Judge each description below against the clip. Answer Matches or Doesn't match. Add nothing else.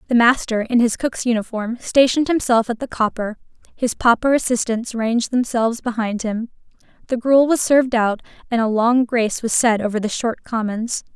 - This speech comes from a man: Doesn't match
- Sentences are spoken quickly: Doesn't match